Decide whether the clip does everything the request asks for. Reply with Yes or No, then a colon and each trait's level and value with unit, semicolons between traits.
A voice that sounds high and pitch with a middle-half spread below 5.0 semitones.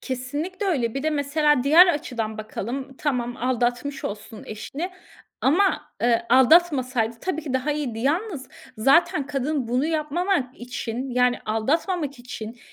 Yes: very high, 270 Hz; average, 3.9 semitones